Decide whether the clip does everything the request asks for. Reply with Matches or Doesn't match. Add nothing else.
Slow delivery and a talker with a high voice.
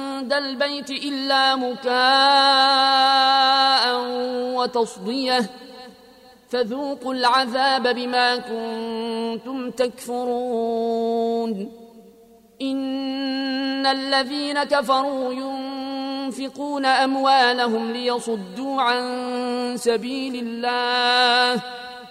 Matches